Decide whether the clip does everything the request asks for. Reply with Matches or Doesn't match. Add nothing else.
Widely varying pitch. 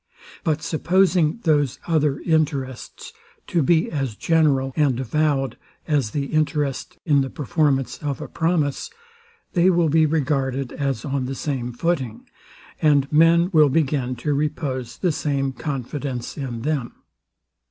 Doesn't match